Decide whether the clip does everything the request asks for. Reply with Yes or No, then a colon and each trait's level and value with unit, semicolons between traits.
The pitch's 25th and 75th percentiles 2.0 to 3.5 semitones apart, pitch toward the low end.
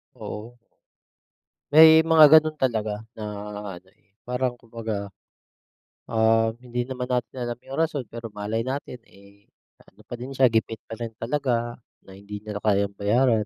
Yes: average, 3.2 semitones; low, 115 Hz